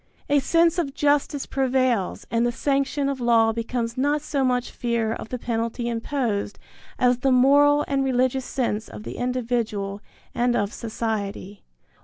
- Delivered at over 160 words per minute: No, average, 155 wpm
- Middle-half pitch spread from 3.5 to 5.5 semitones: No, average, 3.1 semitones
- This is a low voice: No, high, 245 Hz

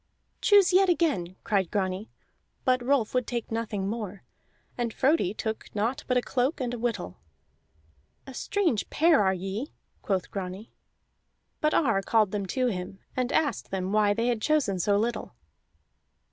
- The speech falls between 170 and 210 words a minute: No, average, 160 wpm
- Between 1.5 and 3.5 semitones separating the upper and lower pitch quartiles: No, average, 4.7 semitones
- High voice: Yes, high, 225 Hz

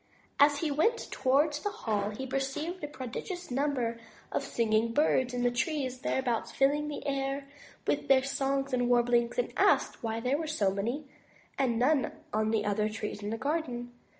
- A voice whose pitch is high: Yes, very high, 260 Hz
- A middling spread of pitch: Yes, average, 3.7 semitones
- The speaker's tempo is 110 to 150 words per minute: No, average, 180 wpm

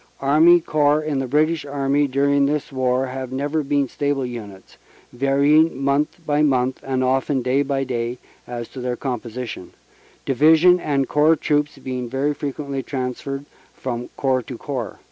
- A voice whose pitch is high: No, low, 135 Hz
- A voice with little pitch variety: Yes, narrow, 2.3 semitones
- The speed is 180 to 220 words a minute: No, average, 155 wpm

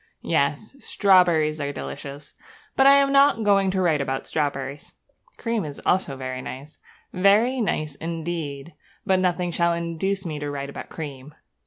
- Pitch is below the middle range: No, medium, 165 Hz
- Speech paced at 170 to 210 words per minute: No, average, 155 wpm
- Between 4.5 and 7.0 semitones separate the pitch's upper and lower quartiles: Yes, average, 5.1 semitones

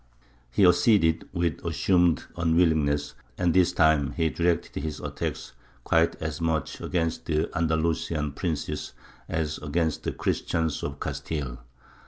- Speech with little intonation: Yes, narrow, 1.9 semitones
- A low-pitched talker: Yes, very low, 80 Hz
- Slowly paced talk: Yes, slow, 125 wpm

